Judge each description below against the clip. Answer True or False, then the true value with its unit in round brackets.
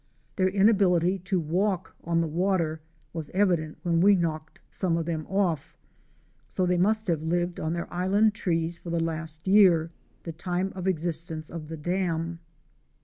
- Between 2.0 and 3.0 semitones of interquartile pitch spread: True (2.6 semitones)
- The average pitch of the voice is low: False (170 Hz)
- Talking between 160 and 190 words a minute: True (165 wpm)